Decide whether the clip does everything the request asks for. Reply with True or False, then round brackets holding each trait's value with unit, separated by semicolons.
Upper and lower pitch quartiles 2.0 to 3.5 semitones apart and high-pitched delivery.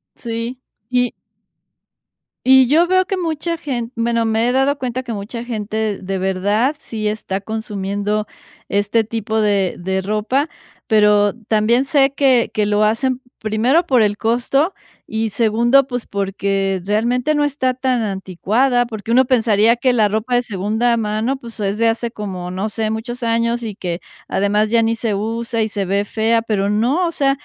True (3.1 semitones; 225 Hz)